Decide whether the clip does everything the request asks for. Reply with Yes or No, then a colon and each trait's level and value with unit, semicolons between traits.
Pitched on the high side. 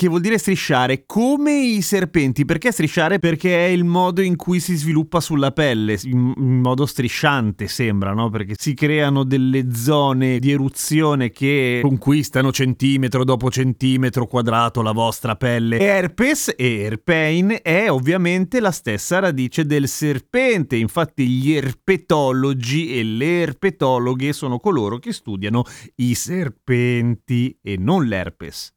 No: low, 135 Hz